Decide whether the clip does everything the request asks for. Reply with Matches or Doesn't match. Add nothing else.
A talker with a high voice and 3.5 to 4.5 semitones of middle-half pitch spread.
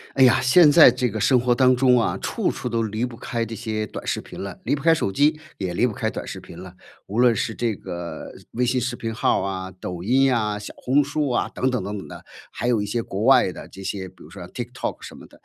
Doesn't match